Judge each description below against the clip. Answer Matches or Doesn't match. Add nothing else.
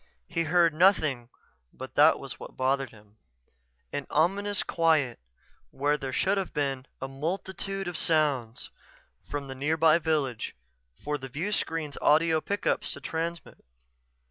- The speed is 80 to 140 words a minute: Matches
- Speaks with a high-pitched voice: Doesn't match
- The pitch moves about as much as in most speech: Matches